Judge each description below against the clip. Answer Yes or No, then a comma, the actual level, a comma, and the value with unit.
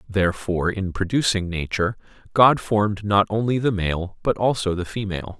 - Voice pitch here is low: Yes, low, 100 Hz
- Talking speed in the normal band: Yes, average, 155 wpm